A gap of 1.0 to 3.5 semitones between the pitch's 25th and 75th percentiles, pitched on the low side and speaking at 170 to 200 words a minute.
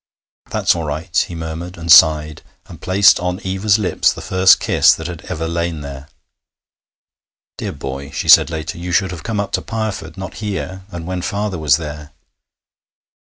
Yes: average, 3.2 semitones; very low, 85 Hz; average, 175 wpm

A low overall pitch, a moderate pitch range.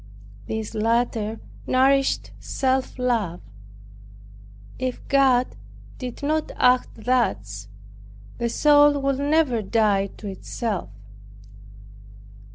No: high, 245 Hz; average, 3.8 semitones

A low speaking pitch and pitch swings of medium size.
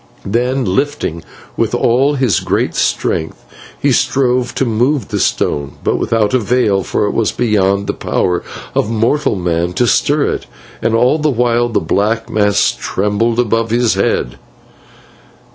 Yes: low, 115 Hz; average, 3.8 semitones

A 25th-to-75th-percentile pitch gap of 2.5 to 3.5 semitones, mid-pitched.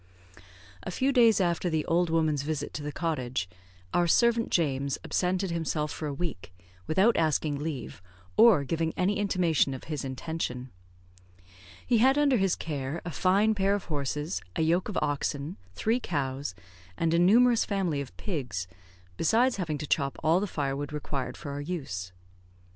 No: average, 4.9 semitones; medium, 160 Hz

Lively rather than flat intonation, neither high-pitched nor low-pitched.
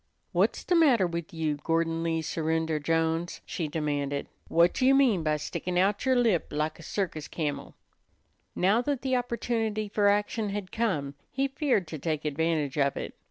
Yes: wide, 5.9 semitones; medium, 170 Hz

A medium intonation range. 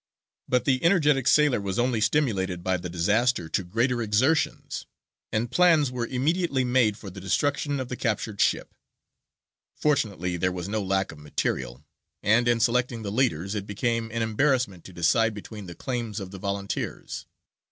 Yes: average, 4.7 semitones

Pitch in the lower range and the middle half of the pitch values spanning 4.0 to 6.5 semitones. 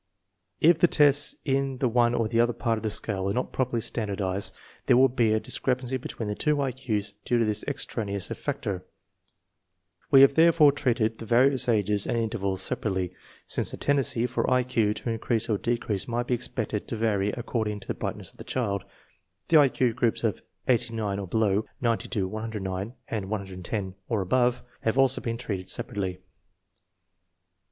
No: low, 115 Hz; average, 3.6 semitones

